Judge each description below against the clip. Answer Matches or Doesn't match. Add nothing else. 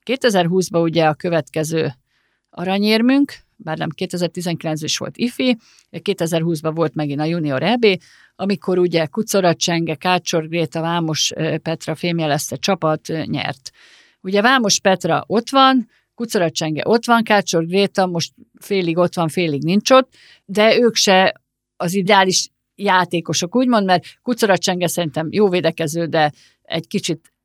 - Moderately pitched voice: Matches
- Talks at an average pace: Matches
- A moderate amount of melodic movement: Matches